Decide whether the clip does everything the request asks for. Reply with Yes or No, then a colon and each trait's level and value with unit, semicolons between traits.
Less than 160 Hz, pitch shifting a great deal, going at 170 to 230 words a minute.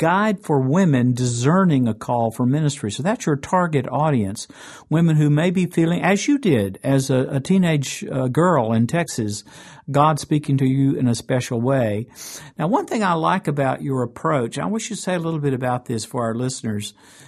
No: medium, 140 Hz; average, 4.9 semitones; average, 200 wpm